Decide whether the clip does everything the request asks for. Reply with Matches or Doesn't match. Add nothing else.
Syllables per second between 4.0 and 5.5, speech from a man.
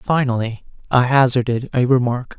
Doesn't match